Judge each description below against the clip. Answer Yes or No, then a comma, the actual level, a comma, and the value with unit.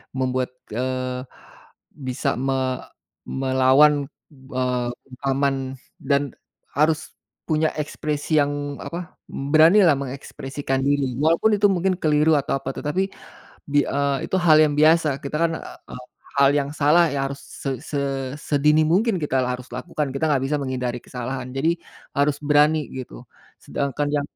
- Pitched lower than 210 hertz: Yes, medium, 140 Hz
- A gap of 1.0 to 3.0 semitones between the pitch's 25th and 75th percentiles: Yes, narrow, 2.6 semitones